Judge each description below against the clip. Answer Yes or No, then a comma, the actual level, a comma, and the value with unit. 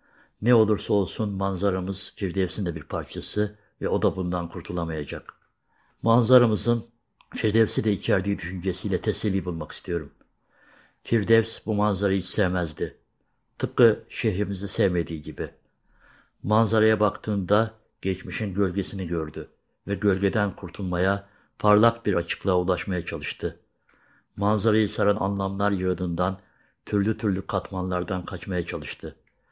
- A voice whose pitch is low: Yes, low, 100 Hz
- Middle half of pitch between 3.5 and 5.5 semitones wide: No, average, 2.7 semitones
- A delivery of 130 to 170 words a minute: No, average, 105 wpm